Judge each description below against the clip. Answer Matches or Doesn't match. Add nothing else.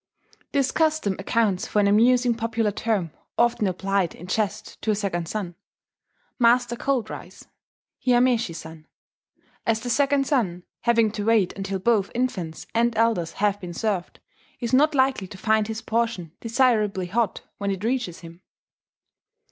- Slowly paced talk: Doesn't match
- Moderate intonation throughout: Matches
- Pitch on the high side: Matches